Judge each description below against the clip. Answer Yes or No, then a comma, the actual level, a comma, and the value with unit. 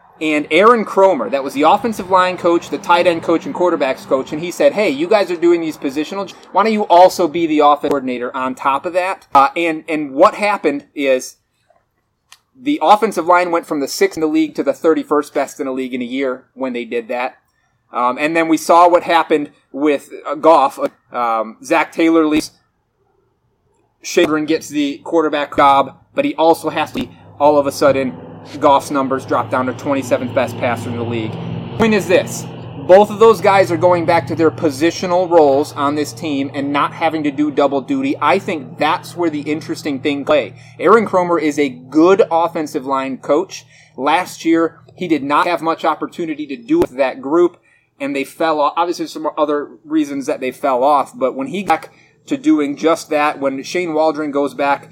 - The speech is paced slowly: No, fast, 205 wpm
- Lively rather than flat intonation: No, average, 4.0 semitones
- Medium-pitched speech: Yes, medium, 155 Hz